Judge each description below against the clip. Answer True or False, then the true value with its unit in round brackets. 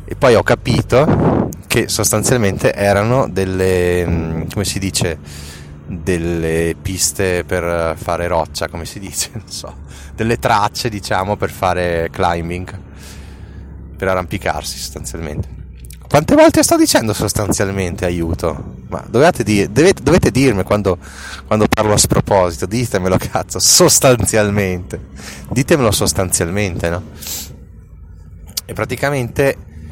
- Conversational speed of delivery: False (110 wpm)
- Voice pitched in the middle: False (90 Hz)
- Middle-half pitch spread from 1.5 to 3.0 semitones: False (4.1 semitones)